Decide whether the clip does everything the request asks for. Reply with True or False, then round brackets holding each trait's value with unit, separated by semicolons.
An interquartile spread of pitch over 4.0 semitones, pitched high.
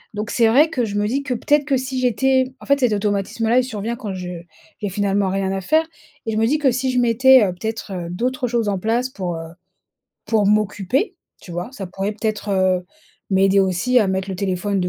True (4.6 semitones; 215 Hz)